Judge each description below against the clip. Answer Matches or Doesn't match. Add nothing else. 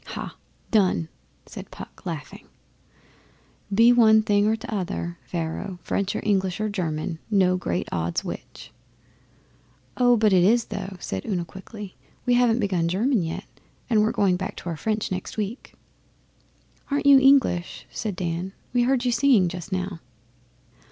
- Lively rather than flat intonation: Doesn't match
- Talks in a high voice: Matches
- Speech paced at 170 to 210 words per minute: Doesn't match